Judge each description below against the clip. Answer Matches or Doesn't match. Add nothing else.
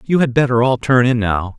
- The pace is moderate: Doesn't match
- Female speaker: Doesn't match